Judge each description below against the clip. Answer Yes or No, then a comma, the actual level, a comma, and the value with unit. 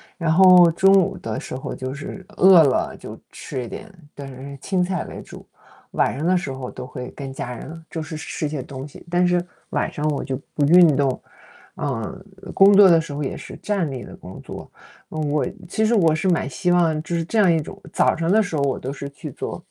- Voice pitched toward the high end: No, medium, 160 Hz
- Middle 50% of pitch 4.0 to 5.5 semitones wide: Yes, average, 4.5 semitones